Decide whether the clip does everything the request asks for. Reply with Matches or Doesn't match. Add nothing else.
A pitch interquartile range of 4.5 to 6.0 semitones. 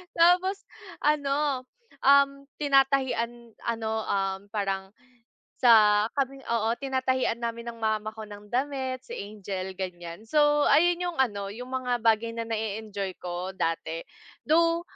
Matches